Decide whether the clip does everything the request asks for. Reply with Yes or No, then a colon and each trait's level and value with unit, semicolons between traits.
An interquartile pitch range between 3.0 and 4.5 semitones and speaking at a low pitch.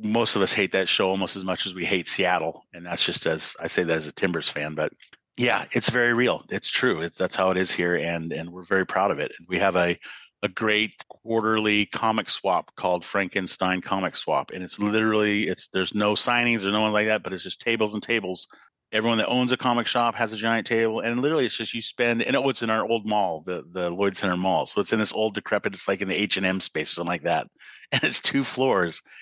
Yes: average, 3.5 semitones; low, 105 Hz